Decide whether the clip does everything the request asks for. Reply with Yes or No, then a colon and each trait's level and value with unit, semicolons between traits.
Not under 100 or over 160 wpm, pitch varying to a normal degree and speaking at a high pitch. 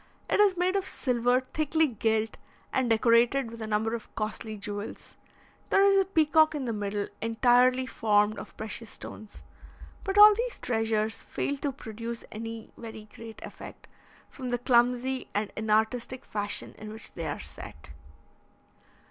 Yes: average, 155 wpm; average, 3.4 semitones; high, 230 Hz